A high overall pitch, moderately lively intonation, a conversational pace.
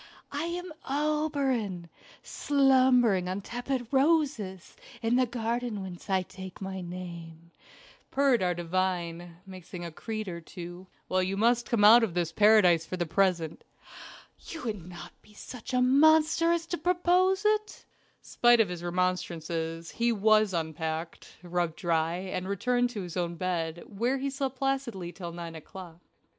No: high, 195 Hz; wide, 6.5 semitones; average, 150 wpm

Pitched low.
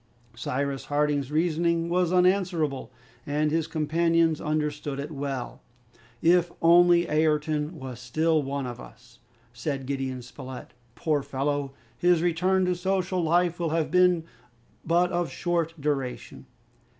No: medium, 155 Hz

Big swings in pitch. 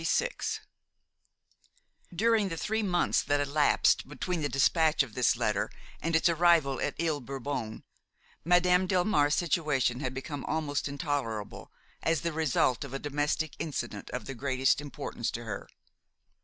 No: average, 3.9 semitones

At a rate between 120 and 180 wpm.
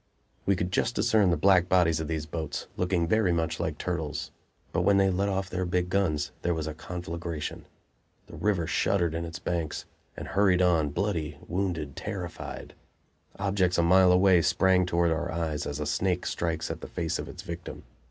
No: average, 190 wpm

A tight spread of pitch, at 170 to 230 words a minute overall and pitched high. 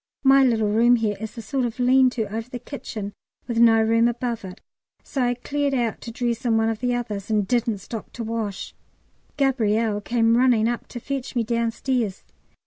Yes: narrow, 1.9 semitones; average, 200 wpm; high, 235 Hz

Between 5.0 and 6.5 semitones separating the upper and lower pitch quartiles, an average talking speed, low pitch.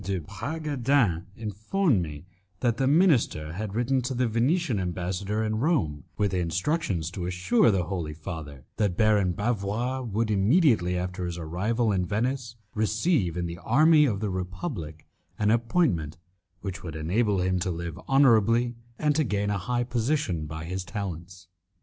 Yes: wide, 5.4 semitones; average, 155 wpm; low, 100 Hz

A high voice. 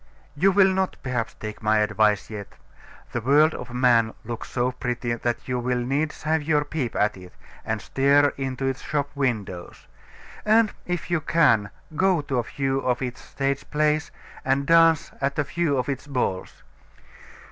No: low, 135 Hz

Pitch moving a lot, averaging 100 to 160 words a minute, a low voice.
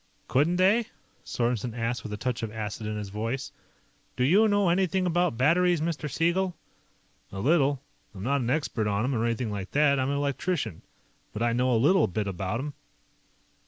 No: wide, 7.1 semitones; average, 190 wpm; low, 130 Hz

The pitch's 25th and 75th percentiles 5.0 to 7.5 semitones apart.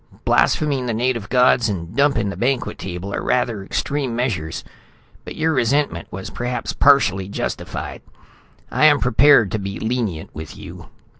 Yes: wide, 5.4 semitones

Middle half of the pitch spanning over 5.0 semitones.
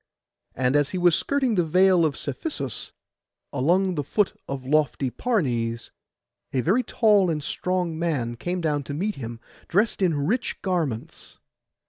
Yes: wide, 5.6 semitones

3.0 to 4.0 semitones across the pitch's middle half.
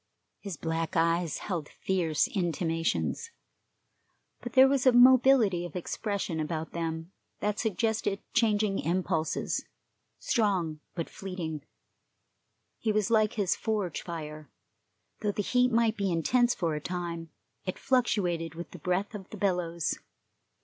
No: average, 4.5 semitones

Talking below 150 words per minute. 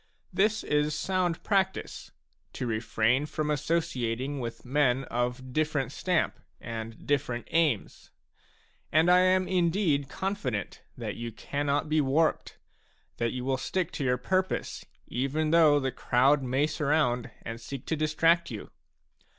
Yes: average, 140 wpm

